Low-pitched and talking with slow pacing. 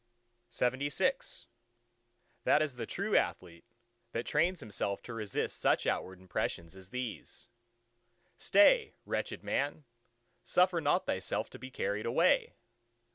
Yes: low, 130 Hz; slow, 120 wpm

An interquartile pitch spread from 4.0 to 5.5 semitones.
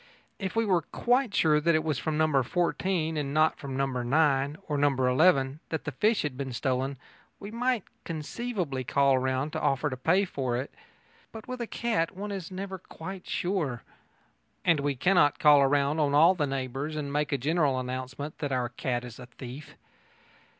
Yes: average, 4.8 semitones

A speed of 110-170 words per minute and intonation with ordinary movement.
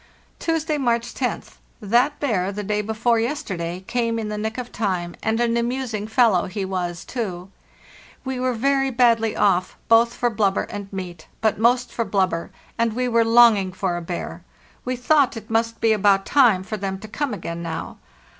No: average, 185 wpm; average, 3.8 semitones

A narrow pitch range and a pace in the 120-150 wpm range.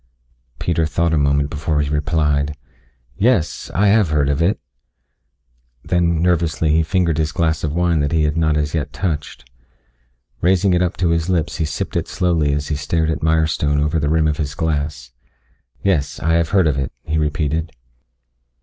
No: narrow, 2.3 semitones; average, 185 wpm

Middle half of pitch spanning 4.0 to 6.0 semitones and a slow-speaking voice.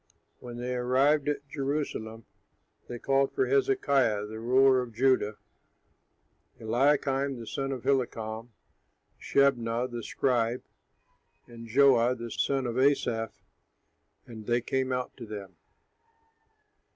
No: average, 2.9 semitones; slow, 115 wpm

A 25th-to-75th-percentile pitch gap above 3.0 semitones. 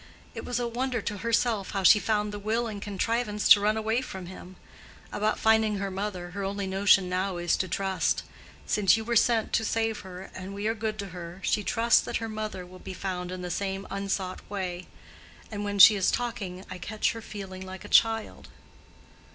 No: average, 2.7 semitones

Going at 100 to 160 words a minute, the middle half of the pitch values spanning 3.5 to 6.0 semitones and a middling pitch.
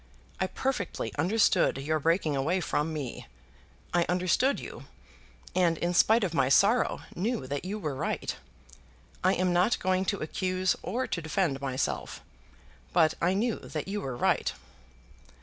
Yes: average, 150 wpm; average, 4.1 semitones; medium, 180 Hz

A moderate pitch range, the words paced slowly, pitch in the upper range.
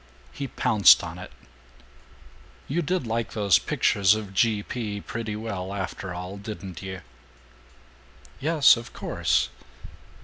No: average, 3.2 semitones; slow, 125 wpm; low, 105 Hz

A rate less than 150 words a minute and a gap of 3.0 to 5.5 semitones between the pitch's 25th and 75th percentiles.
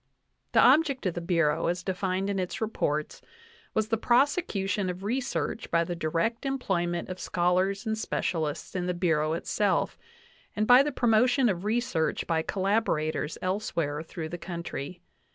No: average, 155 wpm; average, 4.6 semitones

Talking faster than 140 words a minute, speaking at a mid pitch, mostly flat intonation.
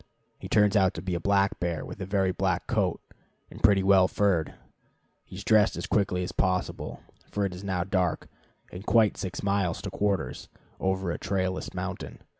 No: average, 190 wpm; very low, 95 Hz; narrow, 1.8 semitones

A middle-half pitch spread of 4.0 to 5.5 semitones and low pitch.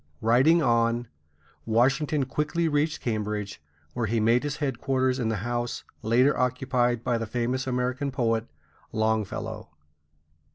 No: average, 2.9 semitones; low, 120 Hz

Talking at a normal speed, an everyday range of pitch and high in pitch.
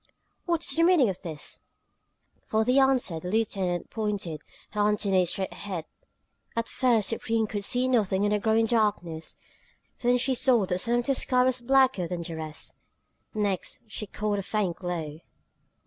Yes: average, 165 wpm; average, 4.8 semitones; high, 210 Hz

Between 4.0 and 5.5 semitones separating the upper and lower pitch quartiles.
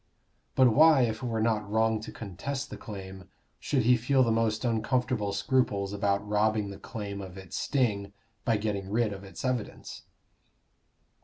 No: average, 3.3 semitones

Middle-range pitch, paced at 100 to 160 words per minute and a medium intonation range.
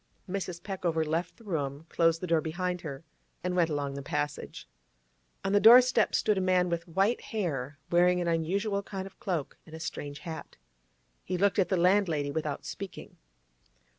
No: medium, 175 Hz; average, 175 wpm; average, 3.4 semitones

